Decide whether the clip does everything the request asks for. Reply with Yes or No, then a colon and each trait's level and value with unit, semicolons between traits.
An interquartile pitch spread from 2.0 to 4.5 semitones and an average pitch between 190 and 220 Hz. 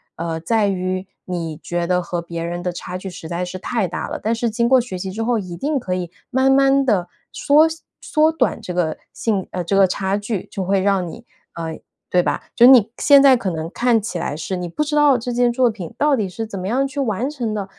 No: wide, 5.5 semitones; high, 200 Hz